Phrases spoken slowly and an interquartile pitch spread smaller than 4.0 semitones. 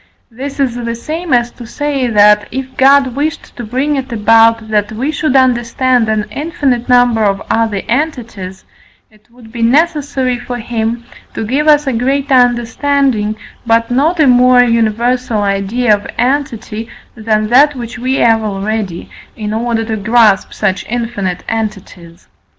No: average, 155 wpm; average, 3.2 semitones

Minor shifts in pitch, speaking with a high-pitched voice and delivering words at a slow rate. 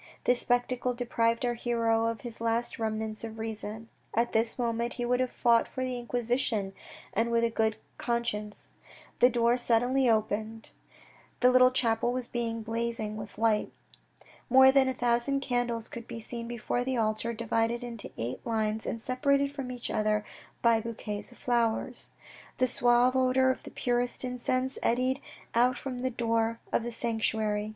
No: narrow, 1.7 semitones; high, 235 Hz; average, 165 wpm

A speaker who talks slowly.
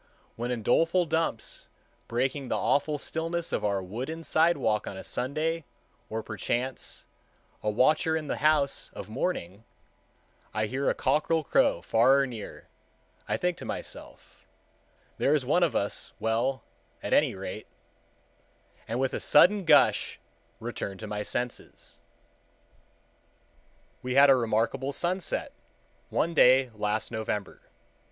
Yes: slow, 130 wpm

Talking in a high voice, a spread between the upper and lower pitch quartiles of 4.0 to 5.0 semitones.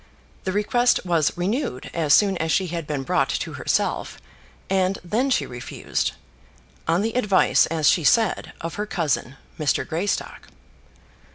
No: medium, 180 Hz; average, 4.5 semitones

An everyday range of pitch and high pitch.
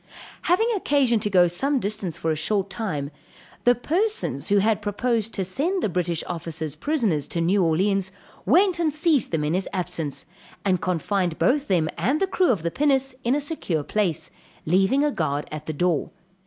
No: wide, 8.3 semitones; high, 195 Hz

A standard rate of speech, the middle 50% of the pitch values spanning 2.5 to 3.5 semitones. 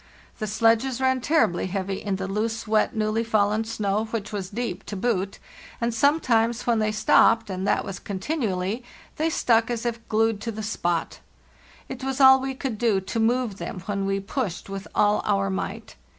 Yes: average, 180 wpm; average, 3.2 semitones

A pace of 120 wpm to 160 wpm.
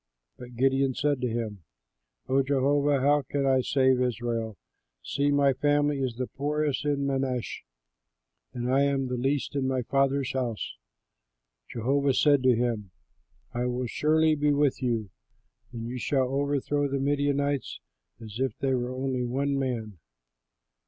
Yes: average, 150 wpm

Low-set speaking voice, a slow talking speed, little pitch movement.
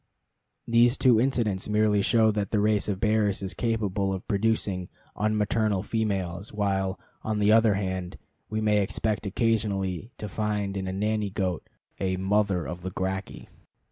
No: low, 105 Hz; average, 155 wpm; narrow, 2.2 semitones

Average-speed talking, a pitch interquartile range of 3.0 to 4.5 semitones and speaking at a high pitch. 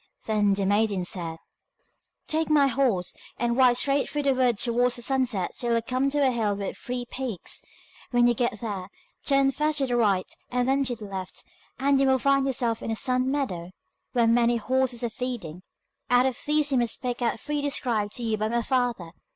No: fast, 210 wpm; average, 3.4 semitones; high, 245 Hz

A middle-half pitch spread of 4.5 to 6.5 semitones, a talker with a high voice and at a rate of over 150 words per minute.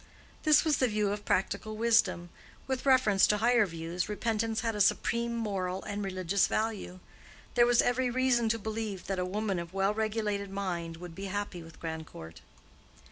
No: average, 3.6 semitones; high, 205 Hz; average, 175 wpm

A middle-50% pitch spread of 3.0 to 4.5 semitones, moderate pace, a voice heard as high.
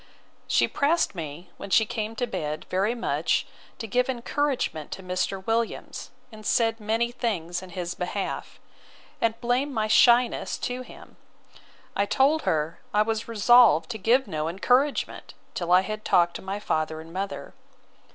No: average, 4.9 semitones; average, 160 wpm; high, 215 Hz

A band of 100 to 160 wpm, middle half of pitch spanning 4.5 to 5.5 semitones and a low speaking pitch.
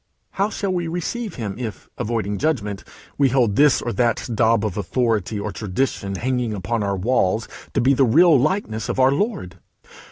No: average, 180 wpm; average, 5.0 semitones; low, 120 Hz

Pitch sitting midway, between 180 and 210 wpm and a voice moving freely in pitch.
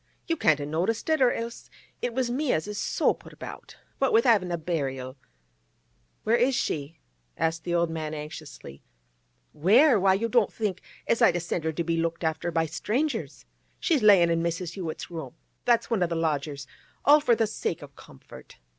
Yes: medium, 175 Hz; average, 190 wpm; wide, 6.3 semitones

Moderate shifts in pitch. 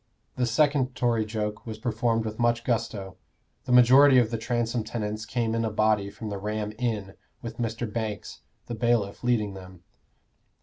No: narrow, 2.1 semitones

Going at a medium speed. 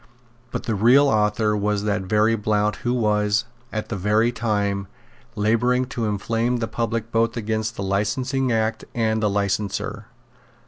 Yes: average, 150 wpm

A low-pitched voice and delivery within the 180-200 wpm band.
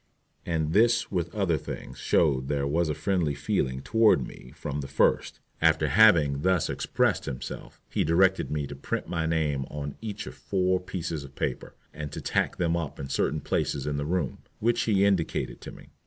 Yes: very low, 80 Hz; average, 190 wpm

